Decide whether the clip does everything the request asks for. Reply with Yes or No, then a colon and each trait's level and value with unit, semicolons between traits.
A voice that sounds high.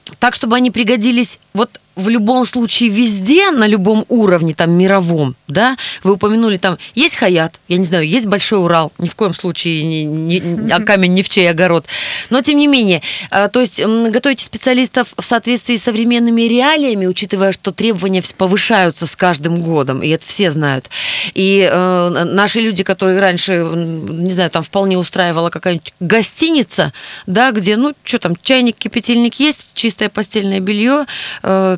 Yes: high, 200 Hz